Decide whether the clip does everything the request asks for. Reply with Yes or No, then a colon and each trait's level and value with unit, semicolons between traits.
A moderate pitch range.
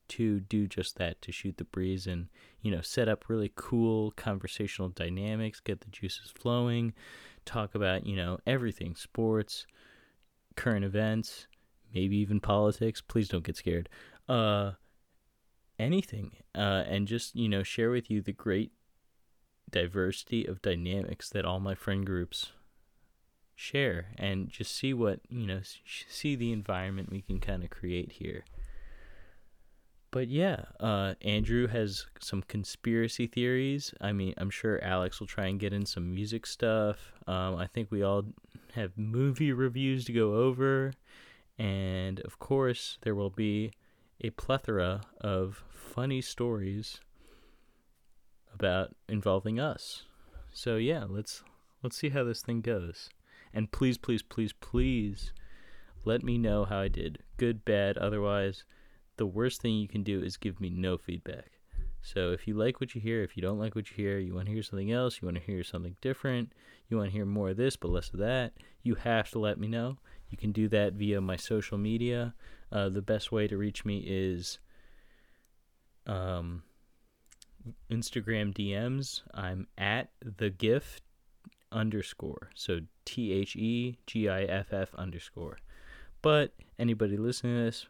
Yes: average, 3.4 semitones